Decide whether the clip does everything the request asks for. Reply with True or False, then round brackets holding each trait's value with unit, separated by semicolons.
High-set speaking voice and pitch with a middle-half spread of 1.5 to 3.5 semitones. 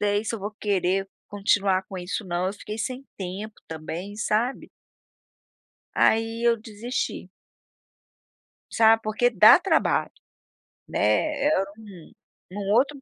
True (210 Hz; 2.7 semitones)